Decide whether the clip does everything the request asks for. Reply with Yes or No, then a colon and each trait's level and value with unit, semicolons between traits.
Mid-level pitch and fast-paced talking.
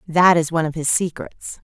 Yes: medium, 165 Hz; fast, 210 wpm